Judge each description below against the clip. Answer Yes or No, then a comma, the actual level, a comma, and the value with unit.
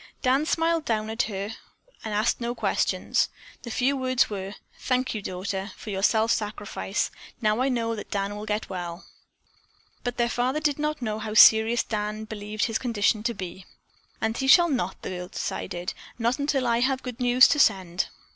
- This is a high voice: Yes, high, 225 Hz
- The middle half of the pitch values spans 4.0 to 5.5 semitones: No, average, 3.5 semitones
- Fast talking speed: No, average, 185 wpm